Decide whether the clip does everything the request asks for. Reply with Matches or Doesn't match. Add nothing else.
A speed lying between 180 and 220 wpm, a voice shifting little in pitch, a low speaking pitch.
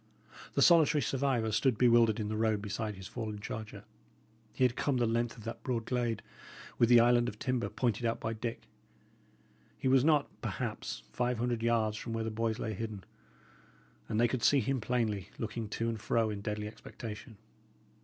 Matches